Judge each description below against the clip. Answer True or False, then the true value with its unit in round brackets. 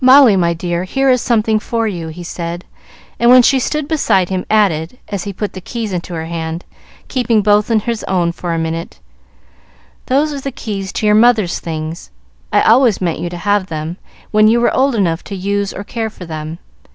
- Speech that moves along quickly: True (210 wpm)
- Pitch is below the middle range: False (200 Hz)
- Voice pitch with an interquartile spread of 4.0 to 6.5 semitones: True (5.2 semitones)